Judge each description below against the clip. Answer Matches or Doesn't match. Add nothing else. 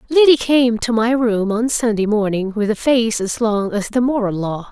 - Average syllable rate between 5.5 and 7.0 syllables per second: Doesn't match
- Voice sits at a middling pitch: Doesn't match